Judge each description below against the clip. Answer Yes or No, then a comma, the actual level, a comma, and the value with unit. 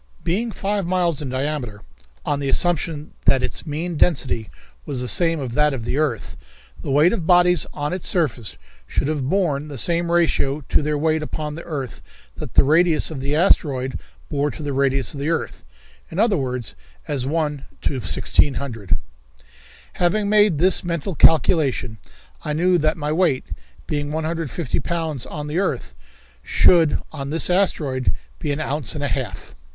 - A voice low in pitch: No, medium, 150 Hz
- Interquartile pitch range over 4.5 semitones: No, average, 3.7 semitones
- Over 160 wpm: Yes, average, 170 wpm